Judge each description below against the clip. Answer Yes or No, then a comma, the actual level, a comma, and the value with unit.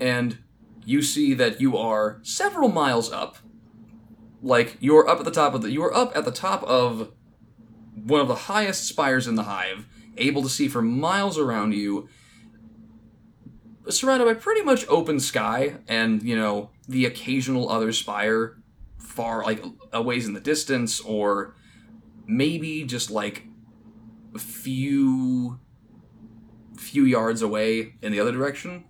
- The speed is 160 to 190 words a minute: No, average, 145 wpm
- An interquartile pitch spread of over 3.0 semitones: Yes, average, 4.1 semitones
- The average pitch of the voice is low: Yes, low, 115 Hz